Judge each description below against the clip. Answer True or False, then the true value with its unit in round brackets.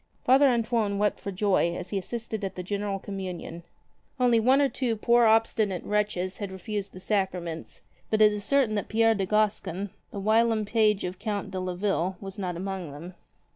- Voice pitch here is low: False (205 Hz)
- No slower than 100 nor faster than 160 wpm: False (190 wpm)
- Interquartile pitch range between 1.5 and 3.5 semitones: True (2.9 semitones)